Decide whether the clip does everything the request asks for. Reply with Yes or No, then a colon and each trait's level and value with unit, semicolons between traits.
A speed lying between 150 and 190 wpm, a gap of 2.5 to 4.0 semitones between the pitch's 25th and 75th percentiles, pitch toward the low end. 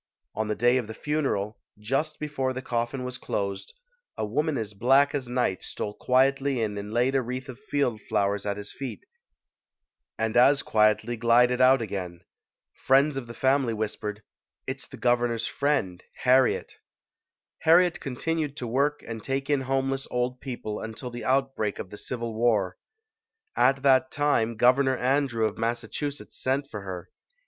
Yes: average, 165 wpm; average, 3.6 semitones; low, 125 Hz